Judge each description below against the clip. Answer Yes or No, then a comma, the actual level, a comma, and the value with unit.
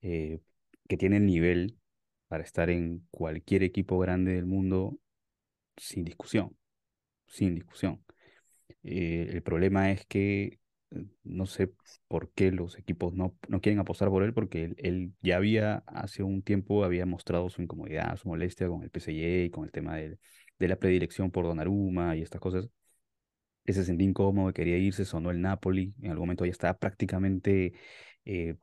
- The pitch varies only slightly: Yes, narrow, 1.9 semitones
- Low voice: Yes, very low, 95 Hz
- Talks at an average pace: Yes, average, 170 wpm